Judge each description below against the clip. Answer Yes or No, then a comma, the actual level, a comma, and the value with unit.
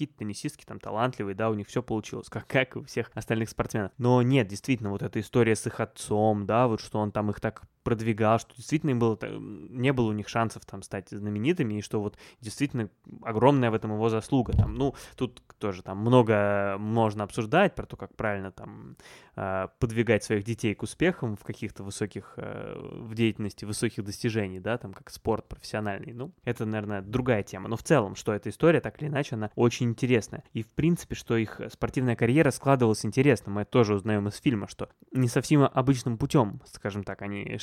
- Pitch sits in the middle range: No, low, 115 Hz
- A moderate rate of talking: No, fast, 195 wpm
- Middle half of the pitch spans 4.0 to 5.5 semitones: No, average, 3.3 semitones